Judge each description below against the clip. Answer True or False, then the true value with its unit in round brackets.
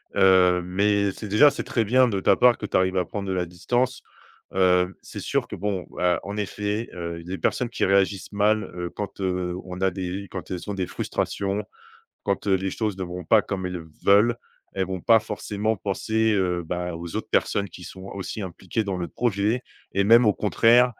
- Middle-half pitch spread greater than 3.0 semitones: False (2.6 semitones)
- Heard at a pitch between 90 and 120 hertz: True (95 Hz)